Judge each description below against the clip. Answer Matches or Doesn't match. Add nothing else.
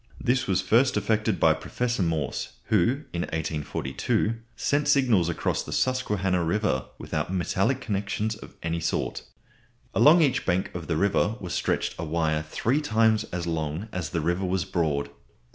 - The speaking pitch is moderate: Doesn't match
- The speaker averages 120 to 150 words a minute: Doesn't match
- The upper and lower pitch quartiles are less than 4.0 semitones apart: Doesn't match